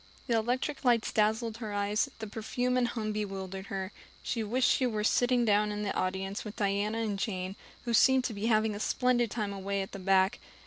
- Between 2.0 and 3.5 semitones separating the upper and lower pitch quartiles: Yes, average, 2.9 semitones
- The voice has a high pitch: Yes, high, 215 Hz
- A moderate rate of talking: No, fast, 210 wpm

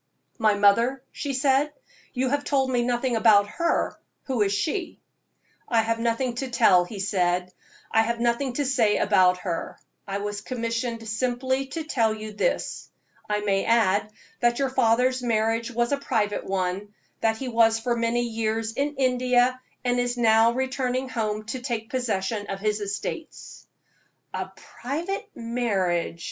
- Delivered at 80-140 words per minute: No, average, 155 wpm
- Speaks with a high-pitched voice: Yes, high, 230 Hz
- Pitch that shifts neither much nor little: Yes, average, 3.3 semitones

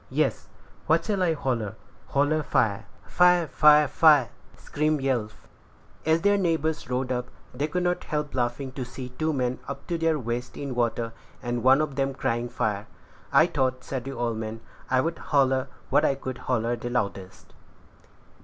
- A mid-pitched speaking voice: No, low, 130 Hz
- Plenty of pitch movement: No, average, 3.9 semitones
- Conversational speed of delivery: Yes, average, 170 wpm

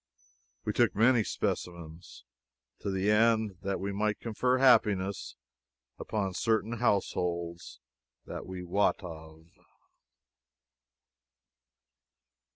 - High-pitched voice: No, low, 100 Hz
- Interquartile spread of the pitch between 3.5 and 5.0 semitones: Yes, average, 3.9 semitones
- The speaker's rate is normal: No, slow, 90 wpm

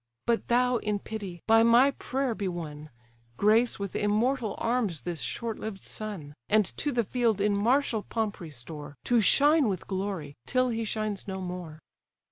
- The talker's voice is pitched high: Yes, high, 210 Hz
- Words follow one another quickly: No, average, 165 wpm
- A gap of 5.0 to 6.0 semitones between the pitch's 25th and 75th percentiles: No, average, 4.3 semitones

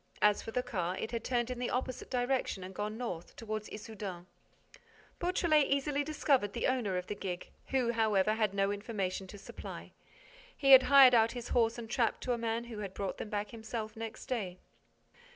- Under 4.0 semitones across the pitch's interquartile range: Yes, average, 3.5 semitones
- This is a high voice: Yes, high, 225 Hz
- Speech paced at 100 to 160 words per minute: No, average, 190 wpm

